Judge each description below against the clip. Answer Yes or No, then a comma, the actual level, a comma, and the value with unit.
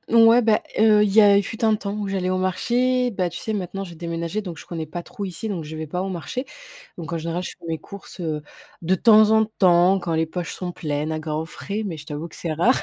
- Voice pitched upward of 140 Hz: Yes, medium, 185 Hz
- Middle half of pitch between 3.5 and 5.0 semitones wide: Yes, average, 4.3 semitones